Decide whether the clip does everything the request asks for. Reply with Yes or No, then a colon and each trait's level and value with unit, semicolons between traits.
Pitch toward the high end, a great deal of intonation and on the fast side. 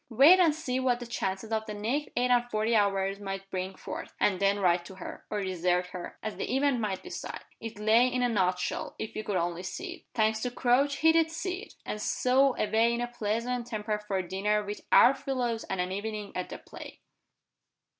No: high, 215 Hz; average, 4.2 semitones; fast, 225 wpm